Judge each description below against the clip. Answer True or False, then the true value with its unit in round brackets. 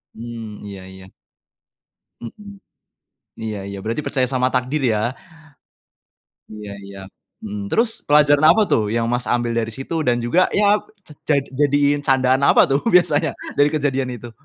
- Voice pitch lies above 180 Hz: False (125 Hz)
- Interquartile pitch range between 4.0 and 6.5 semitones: True (4.6 semitones)